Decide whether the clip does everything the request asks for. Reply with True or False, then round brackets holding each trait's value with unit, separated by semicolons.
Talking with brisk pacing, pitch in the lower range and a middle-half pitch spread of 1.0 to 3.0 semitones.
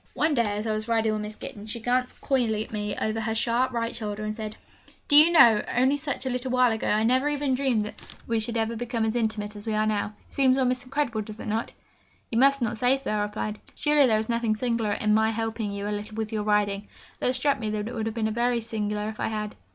False (265 wpm; 225 Hz; 2.7 semitones)